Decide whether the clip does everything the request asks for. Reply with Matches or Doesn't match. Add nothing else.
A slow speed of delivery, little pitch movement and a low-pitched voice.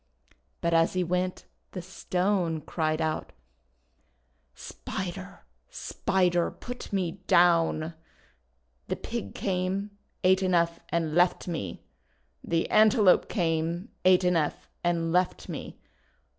Doesn't match